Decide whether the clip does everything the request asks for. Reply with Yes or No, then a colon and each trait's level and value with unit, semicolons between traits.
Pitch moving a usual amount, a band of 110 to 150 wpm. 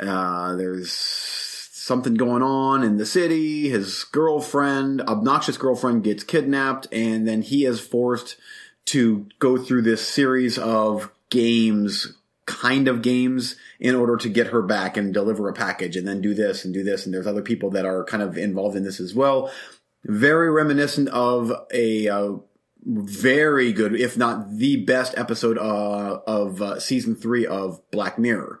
No: average, 4.4 semitones; average, 165 wpm